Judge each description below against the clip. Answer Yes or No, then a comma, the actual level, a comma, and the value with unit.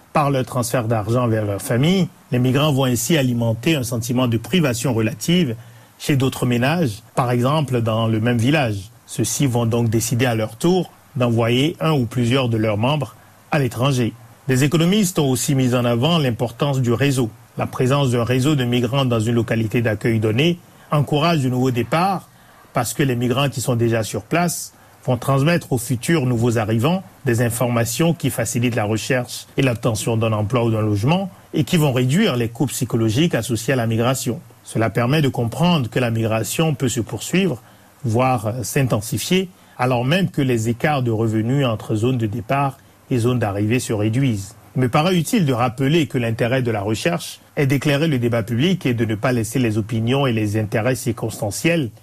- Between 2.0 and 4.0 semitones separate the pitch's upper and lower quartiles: Yes, average, 3.6 semitones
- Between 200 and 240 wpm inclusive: No, average, 185 wpm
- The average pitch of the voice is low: Yes, low, 125 Hz